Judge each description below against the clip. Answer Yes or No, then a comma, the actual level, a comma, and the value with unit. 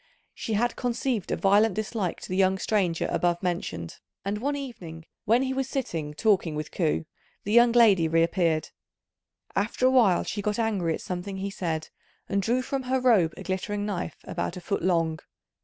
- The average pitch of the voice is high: Yes, high, 200 Hz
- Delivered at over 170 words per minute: Yes, average, 185 wpm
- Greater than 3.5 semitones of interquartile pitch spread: Yes, average, 5.1 semitones